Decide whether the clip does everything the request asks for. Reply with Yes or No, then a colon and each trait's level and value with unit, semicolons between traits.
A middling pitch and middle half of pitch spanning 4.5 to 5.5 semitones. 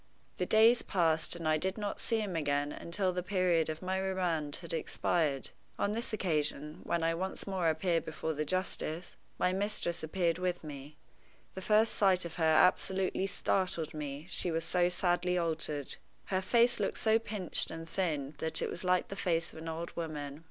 No: medium, 175 Hz; average, 3.0 semitones